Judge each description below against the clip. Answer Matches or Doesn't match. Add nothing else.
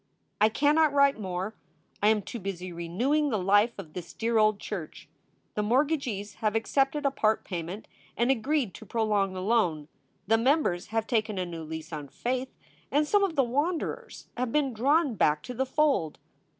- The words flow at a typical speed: Matches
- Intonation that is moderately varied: Doesn't match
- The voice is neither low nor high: Doesn't match